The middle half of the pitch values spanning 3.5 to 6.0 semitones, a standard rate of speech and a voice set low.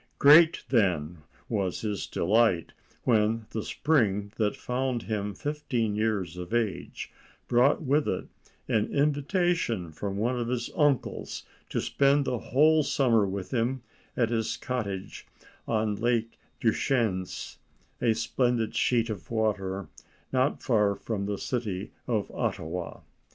No: average, 4.0 semitones; slow, 130 wpm; low, 115 Hz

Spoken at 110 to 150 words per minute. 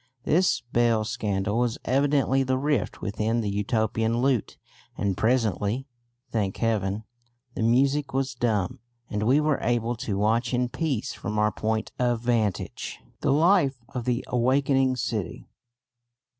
Yes: average, 140 wpm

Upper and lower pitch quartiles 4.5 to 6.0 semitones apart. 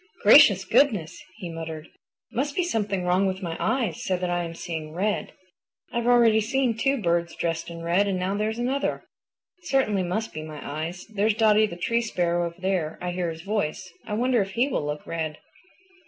Yes: average, 4.8 semitones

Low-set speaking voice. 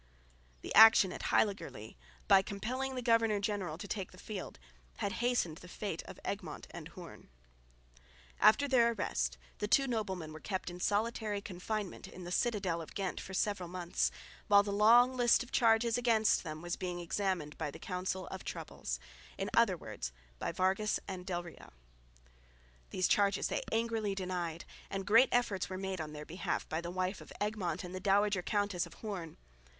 No: high, 195 Hz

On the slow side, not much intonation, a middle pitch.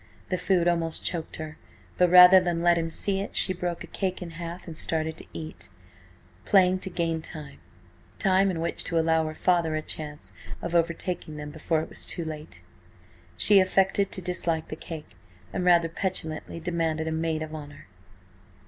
No: average, 185 wpm; narrow, 2.2 semitones; medium, 165 Hz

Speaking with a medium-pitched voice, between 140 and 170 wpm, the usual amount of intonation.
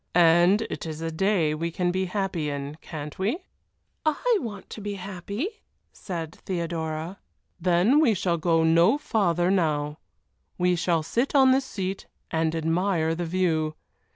Yes: medium, 175 Hz; average, 155 wpm; average, 3.5 semitones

